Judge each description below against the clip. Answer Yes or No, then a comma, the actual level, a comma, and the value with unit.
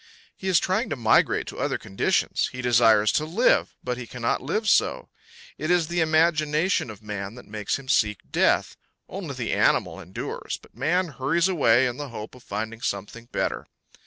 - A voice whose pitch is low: Yes, low, 125 Hz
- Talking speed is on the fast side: No, average, 185 wpm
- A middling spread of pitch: No, wide, 6.4 semitones